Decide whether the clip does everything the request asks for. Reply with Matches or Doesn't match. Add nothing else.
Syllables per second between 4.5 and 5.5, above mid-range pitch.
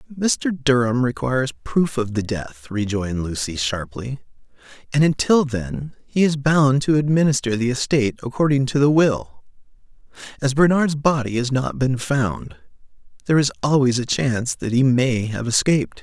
Doesn't match